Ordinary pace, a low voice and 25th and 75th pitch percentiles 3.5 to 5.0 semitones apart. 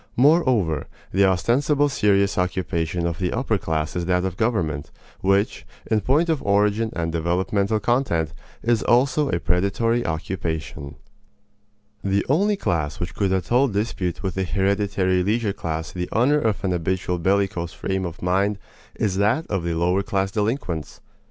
Yes: average, 155 wpm; very low, 95 Hz; average, 4.2 semitones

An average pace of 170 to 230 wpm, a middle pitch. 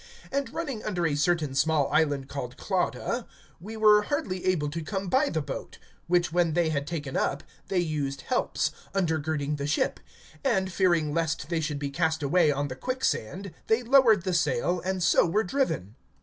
Yes: average, 180 wpm; medium, 170 Hz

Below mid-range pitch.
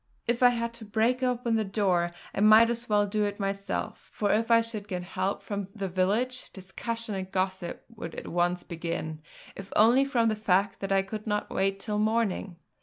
No: high, 205 Hz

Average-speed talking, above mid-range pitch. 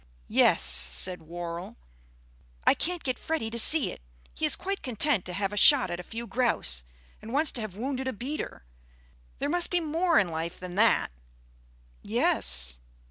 Yes: average, 165 wpm; high, 230 Hz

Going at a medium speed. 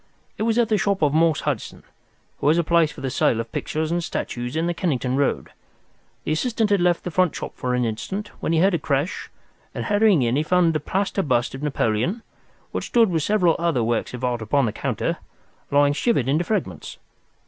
No: fast, 215 wpm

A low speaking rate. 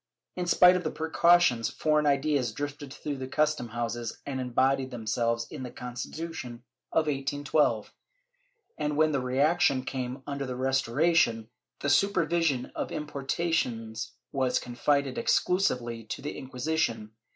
Yes: slow, 130 wpm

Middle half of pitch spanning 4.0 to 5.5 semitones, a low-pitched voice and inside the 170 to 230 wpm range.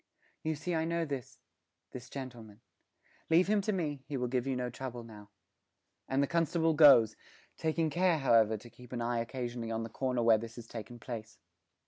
Yes: average, 5.2 semitones; low, 125 Hz; average, 190 wpm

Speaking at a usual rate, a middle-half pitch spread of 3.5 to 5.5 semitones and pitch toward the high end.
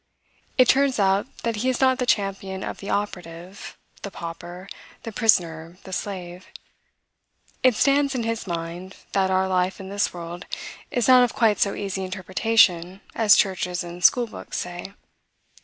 Yes: average, 160 wpm; average, 4.1 semitones; high, 195 Hz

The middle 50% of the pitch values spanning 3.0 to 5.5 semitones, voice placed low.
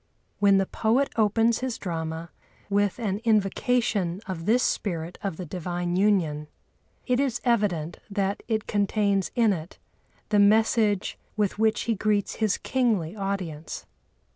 No: average, 3.7 semitones; high, 200 Hz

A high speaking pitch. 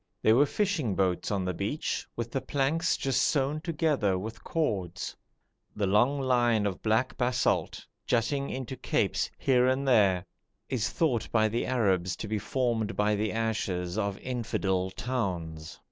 No: low, 115 Hz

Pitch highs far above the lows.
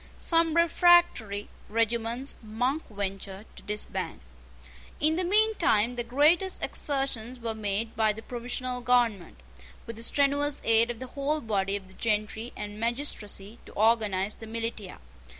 No: average, 4.7 semitones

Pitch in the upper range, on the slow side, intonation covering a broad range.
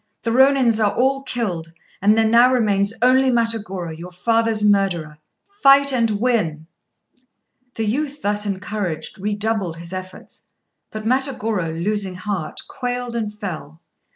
No: high, 210 Hz; slow, 130 wpm; average, 4.3 semitones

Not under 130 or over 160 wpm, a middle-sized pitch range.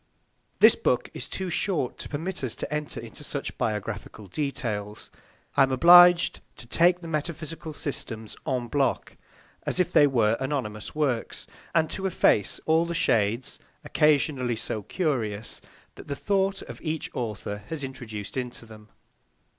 No: average, 150 wpm; wide, 6.3 semitones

